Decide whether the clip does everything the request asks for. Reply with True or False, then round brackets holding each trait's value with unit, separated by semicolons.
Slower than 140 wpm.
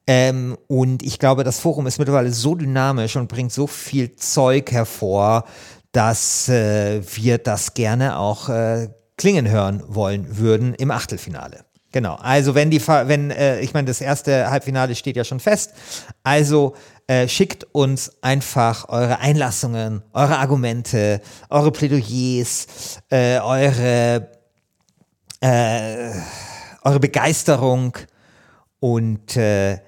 True (125 wpm)